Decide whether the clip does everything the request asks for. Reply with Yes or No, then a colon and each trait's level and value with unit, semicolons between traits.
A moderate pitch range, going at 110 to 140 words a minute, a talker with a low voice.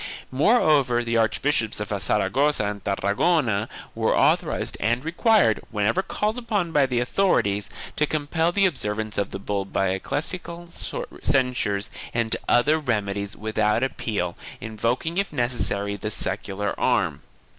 No: wide, 6.9 semitones; slow, 135 wpm; low, 120 Hz